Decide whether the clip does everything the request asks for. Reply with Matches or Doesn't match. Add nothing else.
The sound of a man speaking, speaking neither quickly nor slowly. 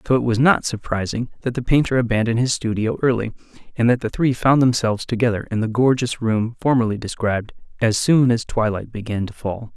Matches